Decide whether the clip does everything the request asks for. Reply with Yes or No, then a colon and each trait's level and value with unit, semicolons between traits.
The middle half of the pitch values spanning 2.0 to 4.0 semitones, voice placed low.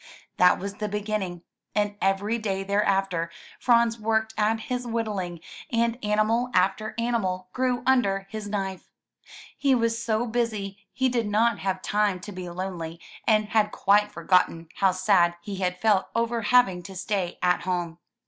No: average, 3.4 semitones; high, 205 Hz